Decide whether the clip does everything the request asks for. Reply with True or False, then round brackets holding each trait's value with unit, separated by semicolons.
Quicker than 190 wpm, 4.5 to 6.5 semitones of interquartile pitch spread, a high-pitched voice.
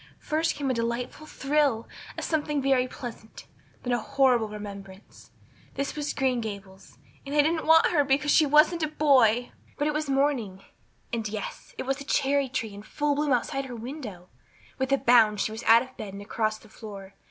True (200 wpm; 4.9 semitones; 255 Hz)